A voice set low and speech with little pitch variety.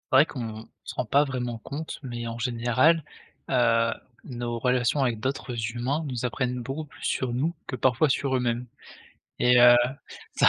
Yes: low, 125 Hz; narrow, 2.1 semitones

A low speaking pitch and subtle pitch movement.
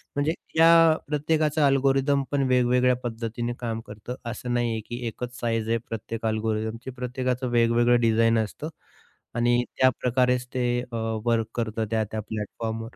Yes: low, 120 Hz; narrow, 2.1 semitones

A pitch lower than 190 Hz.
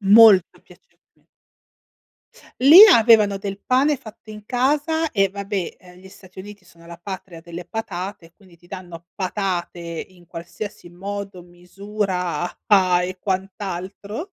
No: high, 195 Hz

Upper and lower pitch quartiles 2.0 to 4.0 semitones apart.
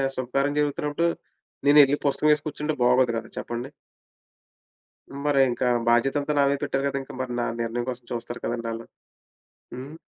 Yes: average, 3.2 semitones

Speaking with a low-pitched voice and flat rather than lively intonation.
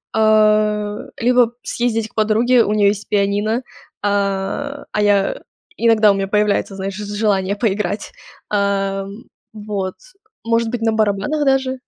No: high, 210 Hz; narrow, 2.1 semitones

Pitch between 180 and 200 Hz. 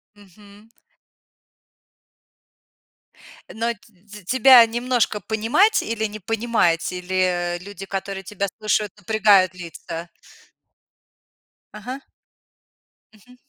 No: high, 210 Hz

